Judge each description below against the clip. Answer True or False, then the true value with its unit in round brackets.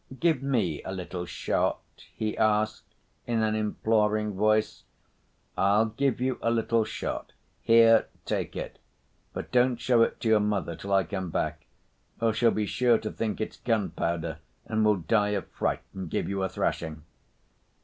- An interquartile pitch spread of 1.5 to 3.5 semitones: True (2.8 semitones)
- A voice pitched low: True (110 Hz)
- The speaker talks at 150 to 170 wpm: True (165 wpm)